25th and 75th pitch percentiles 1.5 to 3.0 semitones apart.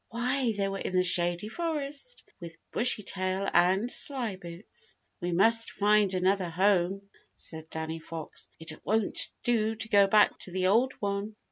No: average, 4.0 semitones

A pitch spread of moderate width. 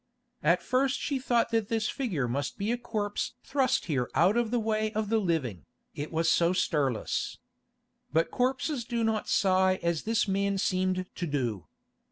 No: wide, 5.9 semitones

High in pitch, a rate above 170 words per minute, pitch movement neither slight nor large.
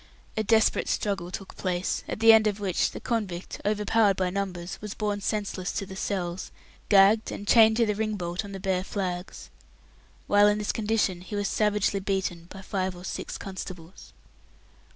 No: high, 200 Hz; average, 180 wpm; narrow, 2.2 semitones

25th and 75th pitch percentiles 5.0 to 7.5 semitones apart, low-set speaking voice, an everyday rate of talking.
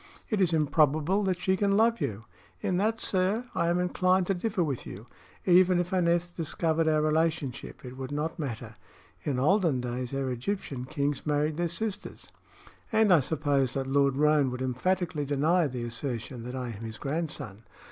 No: average, 5.3 semitones; medium, 155 Hz; average, 175 wpm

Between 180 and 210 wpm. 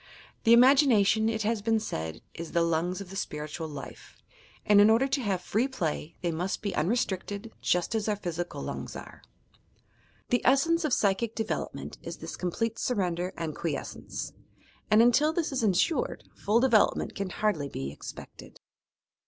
No: average, 165 wpm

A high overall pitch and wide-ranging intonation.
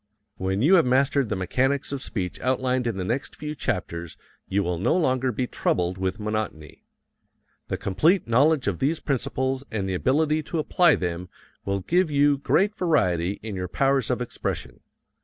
No: low, 125 Hz; wide, 7.0 semitones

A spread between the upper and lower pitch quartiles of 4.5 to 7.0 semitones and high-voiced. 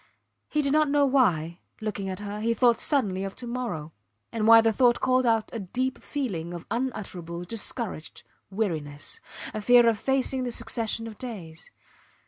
Yes: average, 5.0 semitones; high, 225 Hz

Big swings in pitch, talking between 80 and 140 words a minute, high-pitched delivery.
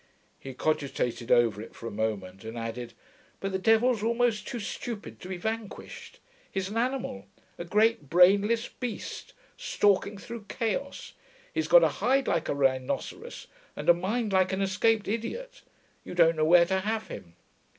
No: wide, 8.1 semitones; average, 165 wpm; high, 195 Hz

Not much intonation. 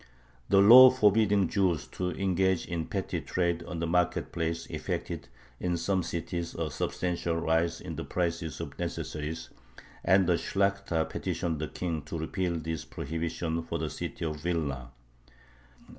Yes: narrow, 2.2 semitones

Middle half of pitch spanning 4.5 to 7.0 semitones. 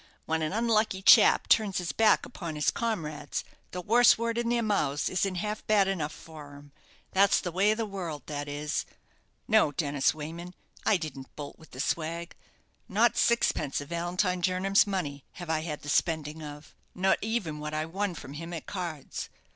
Yes: average, 4.8 semitones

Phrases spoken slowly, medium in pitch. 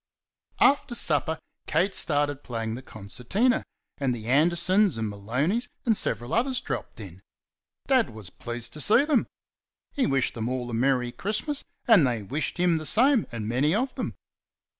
No: average, 160 wpm; medium, 145 Hz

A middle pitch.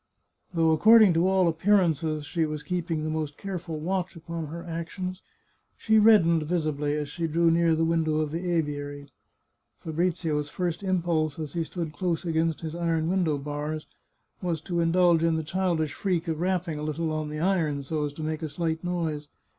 Yes: medium, 165 Hz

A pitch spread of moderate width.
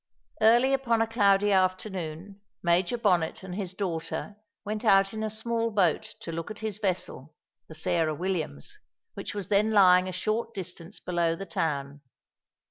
Yes: average, 3.9 semitones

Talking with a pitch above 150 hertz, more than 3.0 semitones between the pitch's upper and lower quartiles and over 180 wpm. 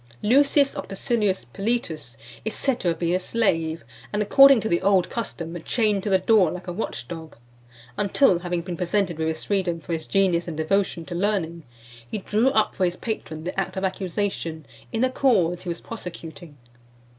Yes: medium, 185 Hz; average, 3.9 semitones; average, 190 wpm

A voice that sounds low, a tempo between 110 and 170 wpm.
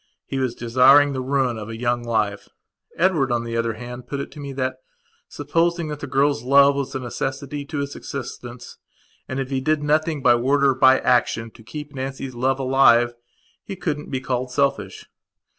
No: low, 130 Hz; average, 195 wpm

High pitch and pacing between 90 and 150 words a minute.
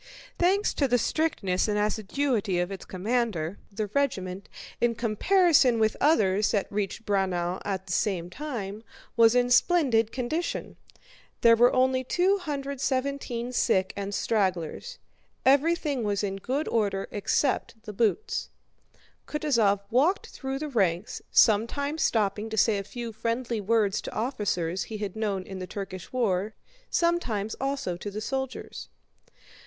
Yes: high, 225 Hz; average, 140 wpm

